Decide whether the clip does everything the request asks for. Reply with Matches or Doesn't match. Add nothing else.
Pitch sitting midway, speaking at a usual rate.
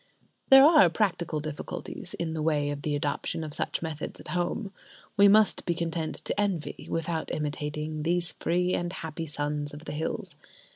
Matches